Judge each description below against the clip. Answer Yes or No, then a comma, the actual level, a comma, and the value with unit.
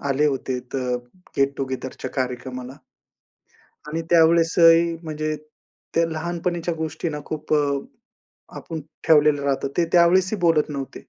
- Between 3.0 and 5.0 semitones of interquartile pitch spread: Yes, average, 3.3 semitones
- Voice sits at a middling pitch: Yes, medium, 155 Hz